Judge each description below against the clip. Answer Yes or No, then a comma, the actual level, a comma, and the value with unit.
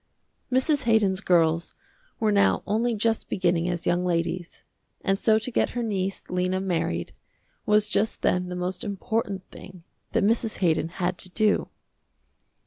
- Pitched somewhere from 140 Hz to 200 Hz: Yes, high, 190 Hz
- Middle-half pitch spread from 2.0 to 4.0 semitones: Yes, average, 3.4 semitones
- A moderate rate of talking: Yes, average, 150 wpm